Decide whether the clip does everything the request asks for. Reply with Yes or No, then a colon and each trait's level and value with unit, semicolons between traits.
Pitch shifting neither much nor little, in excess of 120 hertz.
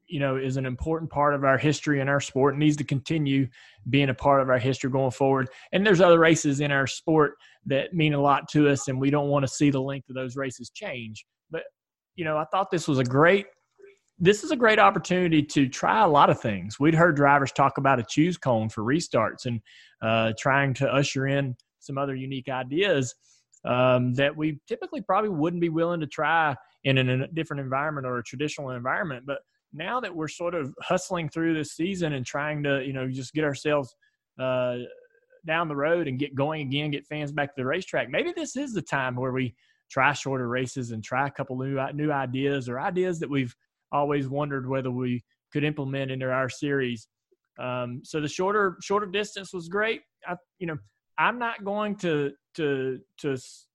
Yes: average, 3.6 semitones; medium, 140 Hz